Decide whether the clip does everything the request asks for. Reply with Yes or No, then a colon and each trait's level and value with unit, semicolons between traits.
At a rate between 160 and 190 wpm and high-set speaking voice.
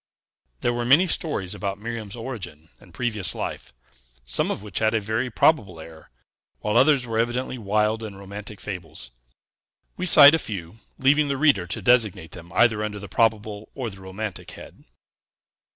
No: average, 170 wpm; low, 110 Hz